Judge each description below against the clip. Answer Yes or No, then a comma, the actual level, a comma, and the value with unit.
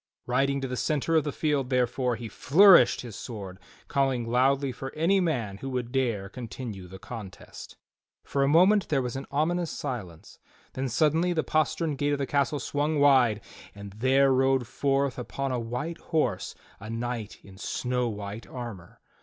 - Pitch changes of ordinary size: Yes, average, 3.7 semitones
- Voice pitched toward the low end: Yes, low, 130 Hz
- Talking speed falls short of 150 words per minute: No, average, 170 wpm